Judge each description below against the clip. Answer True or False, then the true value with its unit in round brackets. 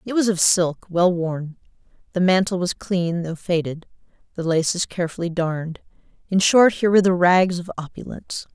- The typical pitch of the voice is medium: True (180 Hz)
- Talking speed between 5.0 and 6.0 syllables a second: True (5.3 syllables/s)